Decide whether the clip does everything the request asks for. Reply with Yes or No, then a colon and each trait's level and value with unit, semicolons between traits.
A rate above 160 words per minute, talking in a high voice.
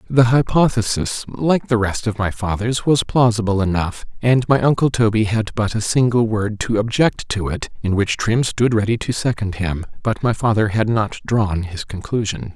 No: average, 180 wpm; low, 110 Hz